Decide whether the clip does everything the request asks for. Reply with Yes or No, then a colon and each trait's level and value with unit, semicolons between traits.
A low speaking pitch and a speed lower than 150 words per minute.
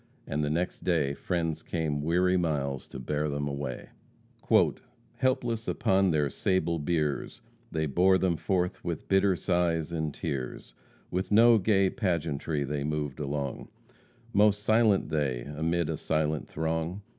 Yes: very low, 80 Hz; average, 140 wpm